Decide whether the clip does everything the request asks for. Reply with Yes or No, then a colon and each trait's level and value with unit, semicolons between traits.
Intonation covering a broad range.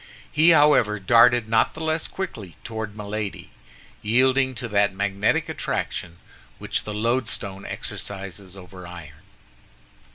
No: average, 4.0 semitones